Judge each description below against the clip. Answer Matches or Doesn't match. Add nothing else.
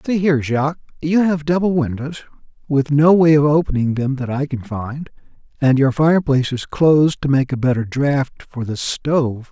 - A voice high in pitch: Doesn't match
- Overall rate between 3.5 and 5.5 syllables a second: Matches